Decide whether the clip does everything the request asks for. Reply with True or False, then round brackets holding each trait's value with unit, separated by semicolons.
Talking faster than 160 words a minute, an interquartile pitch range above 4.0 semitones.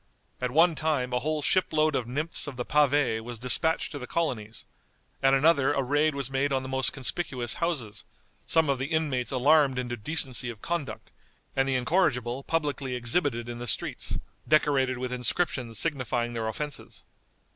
False (175 wpm; 3.5 semitones)